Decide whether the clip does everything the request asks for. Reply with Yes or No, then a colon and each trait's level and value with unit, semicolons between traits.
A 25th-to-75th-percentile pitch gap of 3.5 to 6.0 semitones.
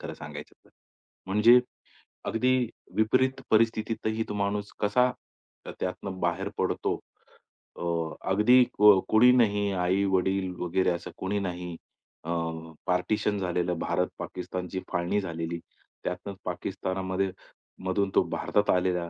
No: average, 2.9 semitones